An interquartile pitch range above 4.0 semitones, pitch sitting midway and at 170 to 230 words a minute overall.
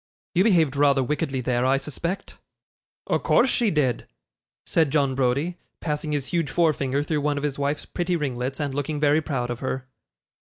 No: average, 3.0 semitones; medium, 145 Hz; average, 180 wpm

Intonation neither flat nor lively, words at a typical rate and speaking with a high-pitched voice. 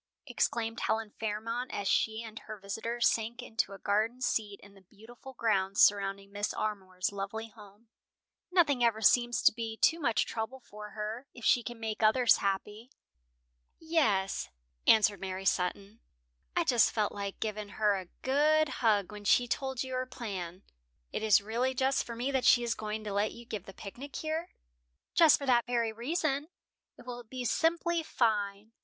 Yes: average, 3.3 semitones; average, 175 wpm; high, 225 Hz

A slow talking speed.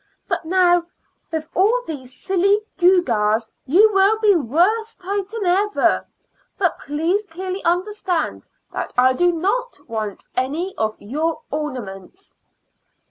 Yes: slow, 120 wpm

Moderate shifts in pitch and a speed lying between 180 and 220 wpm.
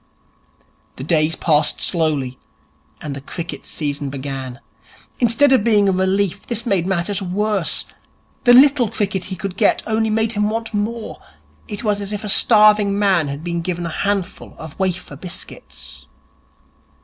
No: average, 4.5 semitones; average, 155 wpm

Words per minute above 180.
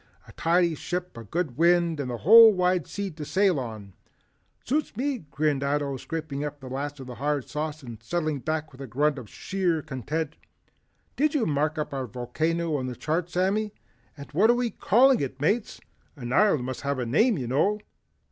Yes: average, 195 wpm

